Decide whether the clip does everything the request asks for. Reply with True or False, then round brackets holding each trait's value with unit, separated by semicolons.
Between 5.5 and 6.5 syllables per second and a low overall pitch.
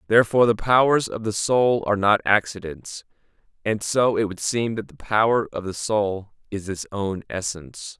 False (5.0 syllables/s; 105 Hz)